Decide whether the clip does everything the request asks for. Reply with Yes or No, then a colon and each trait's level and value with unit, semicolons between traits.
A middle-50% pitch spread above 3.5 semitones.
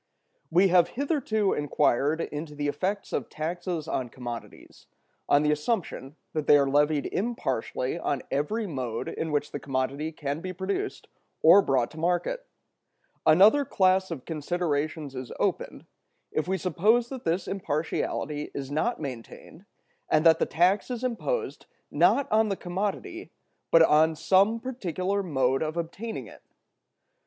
Yes: average, 5.1 semitones